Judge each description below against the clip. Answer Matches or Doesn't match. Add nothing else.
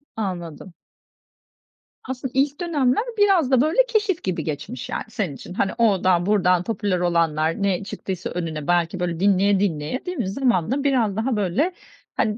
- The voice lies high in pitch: Matches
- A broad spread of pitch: Matches